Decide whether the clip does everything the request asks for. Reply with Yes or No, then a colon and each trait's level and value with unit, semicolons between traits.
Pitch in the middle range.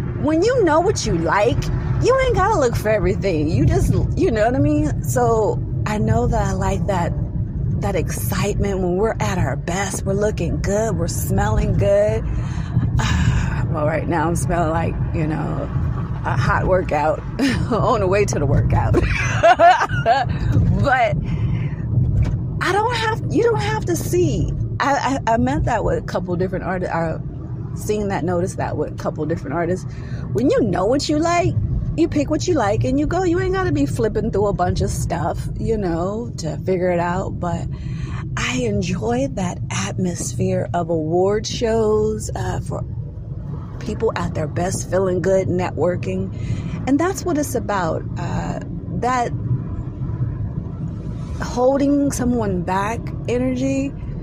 Yes: medium, 165 Hz